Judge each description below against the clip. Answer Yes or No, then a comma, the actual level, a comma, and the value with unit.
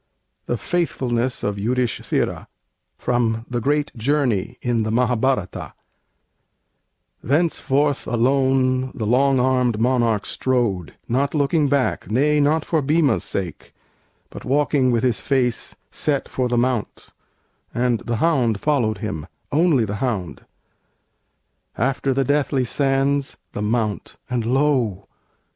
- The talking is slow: Yes, slow, 120 wpm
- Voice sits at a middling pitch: No, low, 125 Hz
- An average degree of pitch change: Yes, average, 3.3 semitones